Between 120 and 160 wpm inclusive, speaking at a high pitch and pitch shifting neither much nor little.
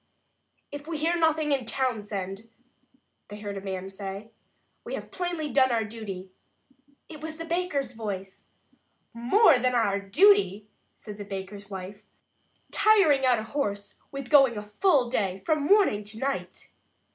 No: average, 150 wpm; high, 235 Hz; wide, 6.8 semitones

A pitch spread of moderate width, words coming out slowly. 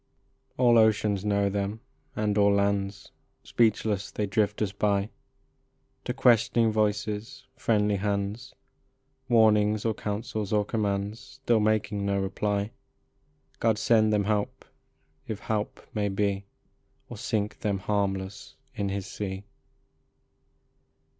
No: narrow, 1.4 semitones; slow, 115 wpm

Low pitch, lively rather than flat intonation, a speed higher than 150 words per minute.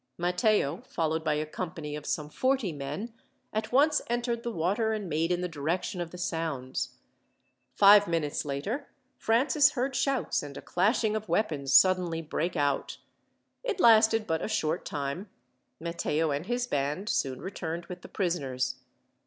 No: medium, 175 Hz; wide, 6.2 semitones; average, 160 wpm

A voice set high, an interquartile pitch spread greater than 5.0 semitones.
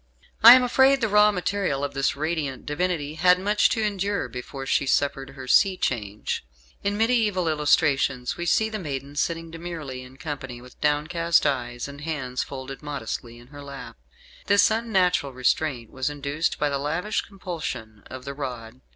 No: medium, 150 Hz; wide, 5.5 semitones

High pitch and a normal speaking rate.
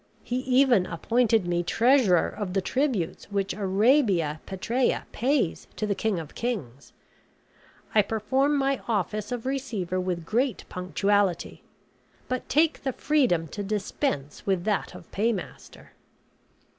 No: high, 210 Hz; slow, 130 wpm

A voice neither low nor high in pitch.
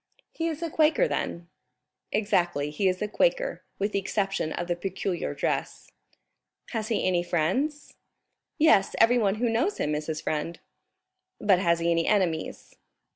No: high, 195 Hz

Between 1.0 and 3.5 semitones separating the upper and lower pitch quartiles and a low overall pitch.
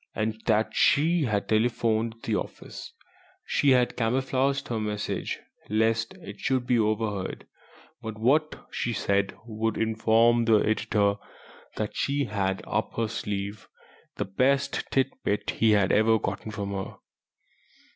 Yes: average, 2.7 semitones; low, 110 Hz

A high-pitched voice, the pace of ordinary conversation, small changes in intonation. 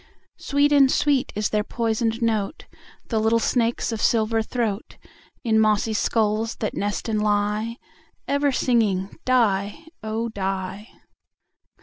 No: high, 220 Hz; slow, 125 wpm; narrow, 2.0 semitones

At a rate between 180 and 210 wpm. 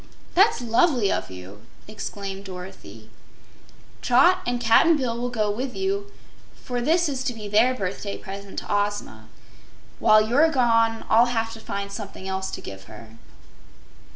No: average, 155 wpm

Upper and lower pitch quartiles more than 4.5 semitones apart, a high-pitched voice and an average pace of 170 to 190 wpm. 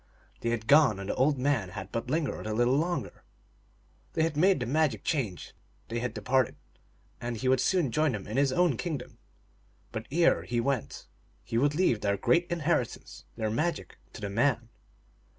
No: average, 5.1 semitones; low, 130 Hz; average, 185 wpm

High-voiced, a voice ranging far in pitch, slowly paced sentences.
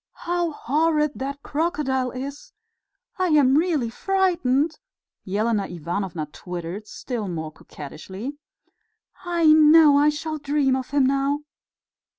Yes: very high, 280 Hz; wide, 5.7 semitones; slow, 115 wpm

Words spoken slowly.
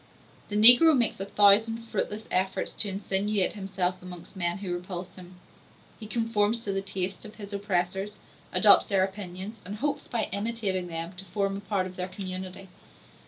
No: average, 170 wpm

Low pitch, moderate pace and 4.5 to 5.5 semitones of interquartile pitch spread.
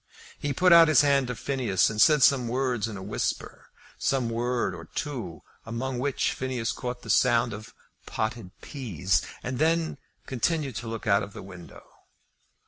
No: low, 125 Hz; average, 170 wpm; average, 4.0 semitones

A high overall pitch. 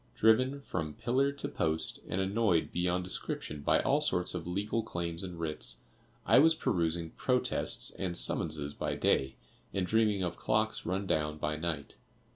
No: very low, 90 Hz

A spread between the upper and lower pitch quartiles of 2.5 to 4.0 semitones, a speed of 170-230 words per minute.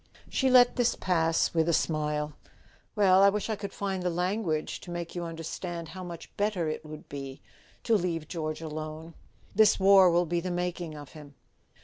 Yes: average, 3.5 semitones; average, 190 wpm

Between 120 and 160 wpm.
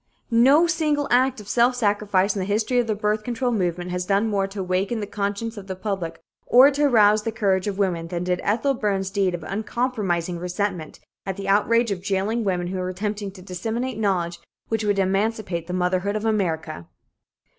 No: average, 200 wpm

